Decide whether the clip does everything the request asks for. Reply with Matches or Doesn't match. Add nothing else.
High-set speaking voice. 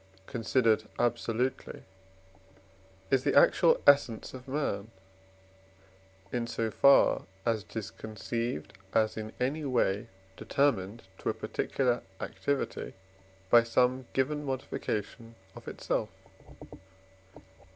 Doesn't match